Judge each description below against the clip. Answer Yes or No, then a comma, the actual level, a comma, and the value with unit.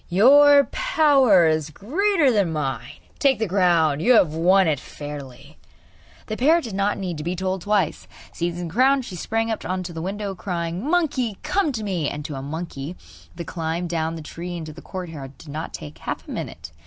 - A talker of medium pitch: Yes, medium, 180 Hz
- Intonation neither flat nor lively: No, wide, 5.9 semitones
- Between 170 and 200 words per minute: Yes, average, 195 wpm